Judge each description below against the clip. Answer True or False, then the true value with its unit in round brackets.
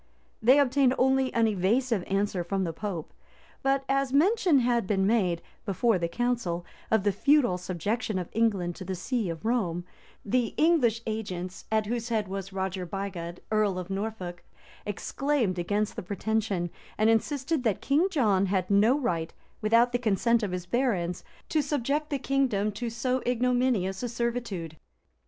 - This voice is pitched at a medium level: False (220 Hz)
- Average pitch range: True (4.9 semitones)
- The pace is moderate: True (165 wpm)